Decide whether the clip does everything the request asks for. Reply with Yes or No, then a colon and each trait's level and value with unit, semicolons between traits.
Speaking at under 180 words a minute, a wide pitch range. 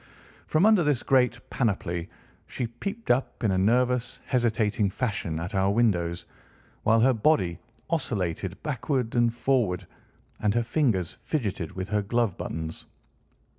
No: slow, 135 wpm; average, 4.9 semitones